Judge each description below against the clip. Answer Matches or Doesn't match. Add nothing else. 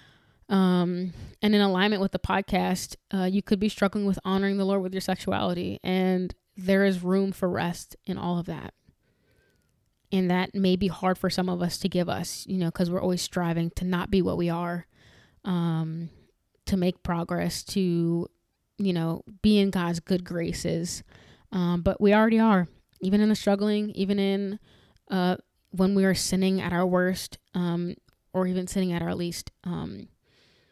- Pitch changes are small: Matches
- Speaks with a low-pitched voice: Doesn't match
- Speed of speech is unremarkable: Matches